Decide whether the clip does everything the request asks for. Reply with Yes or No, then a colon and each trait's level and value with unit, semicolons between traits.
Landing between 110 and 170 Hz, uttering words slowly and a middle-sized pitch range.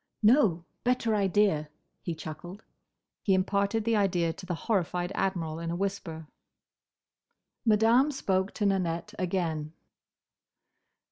No: high, 190 Hz; slow, 115 wpm; average, 3.8 semitones